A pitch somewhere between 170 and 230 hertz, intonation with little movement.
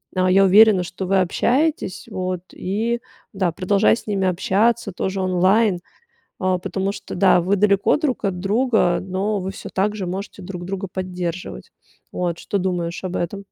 Yes: high, 190 Hz; narrow, 2.0 semitones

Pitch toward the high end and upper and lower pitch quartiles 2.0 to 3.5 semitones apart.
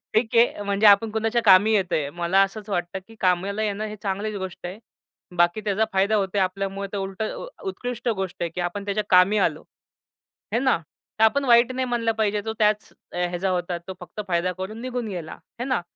Yes: high, 200 Hz; average, 2.9 semitones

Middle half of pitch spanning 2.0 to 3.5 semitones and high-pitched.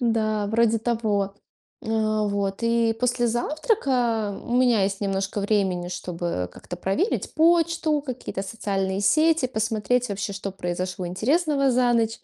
No: average, 4.1 semitones; high, 220 Hz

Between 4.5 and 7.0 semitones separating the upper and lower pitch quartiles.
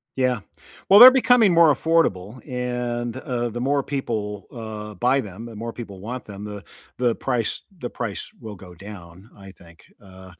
No: average, 3.9 semitones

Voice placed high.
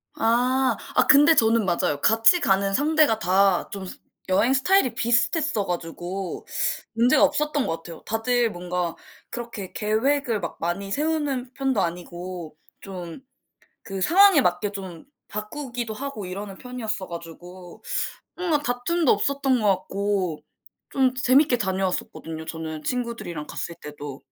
Yes: high, 215 Hz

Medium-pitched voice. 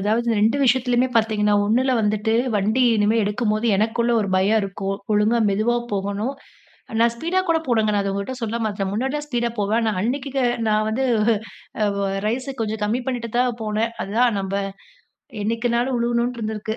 No: high, 220 Hz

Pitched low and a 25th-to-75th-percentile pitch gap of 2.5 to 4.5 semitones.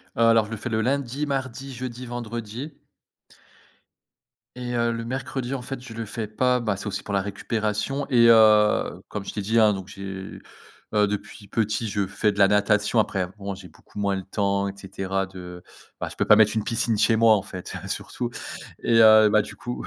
Yes: low, 110 Hz; average, 2.8 semitones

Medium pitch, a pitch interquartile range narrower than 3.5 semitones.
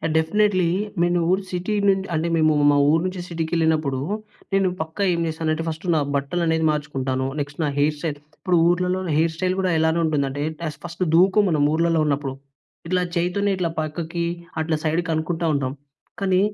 Yes: medium, 165 Hz; narrow, 2.5 semitones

